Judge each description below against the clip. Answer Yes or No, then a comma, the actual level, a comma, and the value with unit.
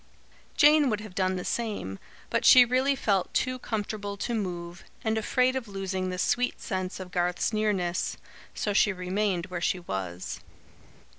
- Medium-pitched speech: No, high, 200 Hz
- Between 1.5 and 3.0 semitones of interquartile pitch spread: No, average, 3.6 semitones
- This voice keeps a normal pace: Yes, average, 160 wpm